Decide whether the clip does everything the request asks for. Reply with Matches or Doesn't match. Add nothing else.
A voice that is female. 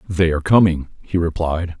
Doesn't match